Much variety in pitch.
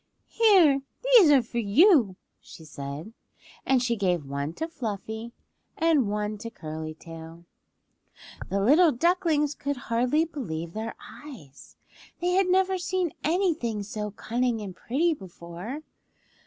Yes: wide, 8.8 semitones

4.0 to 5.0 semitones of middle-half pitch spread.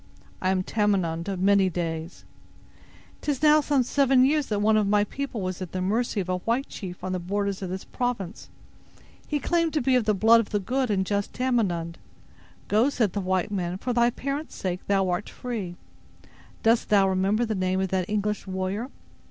Yes: average, 4.5 semitones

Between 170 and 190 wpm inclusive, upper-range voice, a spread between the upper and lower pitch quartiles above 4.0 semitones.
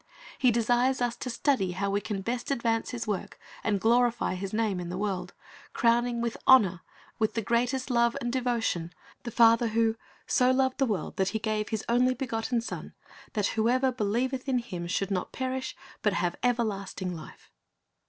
No: average, 180 wpm; high, 230 Hz; average, 3.5 semitones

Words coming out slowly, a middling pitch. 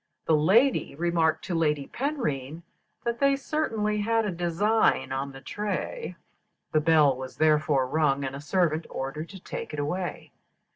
No: average, 155 wpm; medium, 165 Hz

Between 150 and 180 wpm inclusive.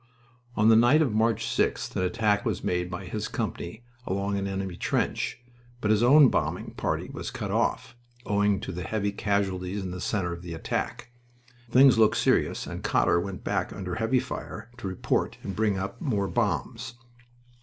Yes: average, 175 wpm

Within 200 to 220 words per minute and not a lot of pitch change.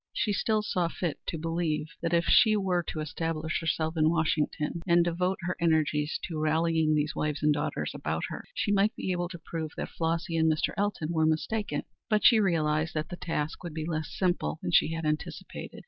Yes: fast, 205 wpm; narrow, 2.2 semitones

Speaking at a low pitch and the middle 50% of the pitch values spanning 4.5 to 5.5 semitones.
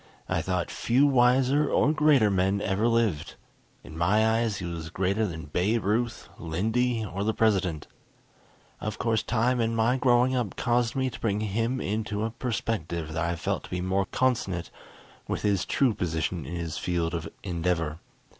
Yes: low, 105 Hz; average, 5.0 semitones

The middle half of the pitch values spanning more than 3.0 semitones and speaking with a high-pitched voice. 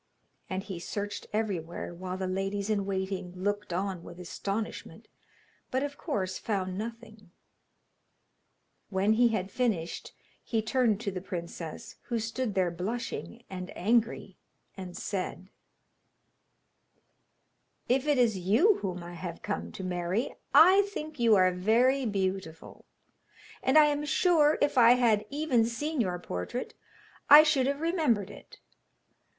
Yes: average, 5.0 semitones; high, 205 Hz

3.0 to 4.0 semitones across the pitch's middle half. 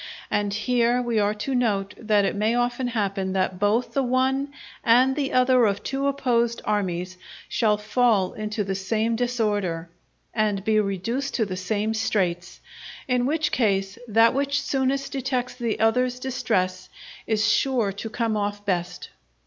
Yes: average, 3.7 semitones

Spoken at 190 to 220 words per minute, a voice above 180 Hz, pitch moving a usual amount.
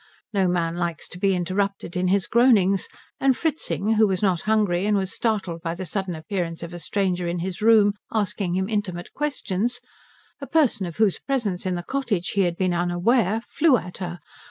Yes: average, 195 wpm; high, 190 Hz; average, 3.6 semitones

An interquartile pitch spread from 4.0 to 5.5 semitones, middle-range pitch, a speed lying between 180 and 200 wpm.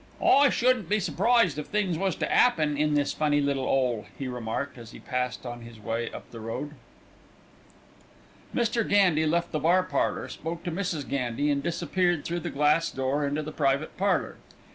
Yes: average, 4.8 semitones; medium, 150 Hz; average, 185 wpm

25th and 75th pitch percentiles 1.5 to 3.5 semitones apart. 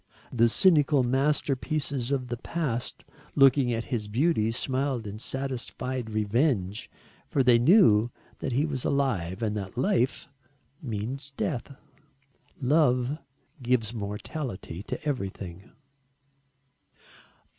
No: average, 3.9 semitones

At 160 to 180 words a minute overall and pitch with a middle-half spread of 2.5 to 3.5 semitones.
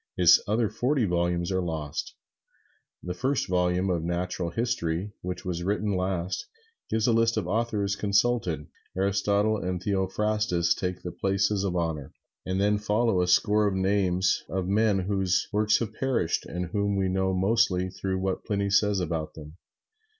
Yes: average, 165 wpm; average, 2.8 semitones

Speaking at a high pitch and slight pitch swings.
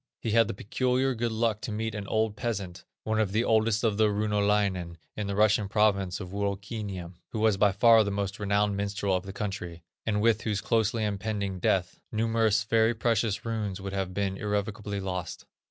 No: low, 105 Hz; narrow, 2.1 semitones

